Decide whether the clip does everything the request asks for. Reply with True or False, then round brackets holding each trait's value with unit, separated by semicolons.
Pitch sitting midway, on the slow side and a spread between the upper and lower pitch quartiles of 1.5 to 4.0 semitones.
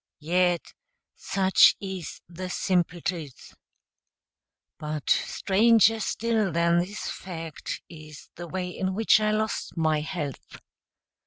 True (180 Hz; 110 wpm; 3.1 semitones)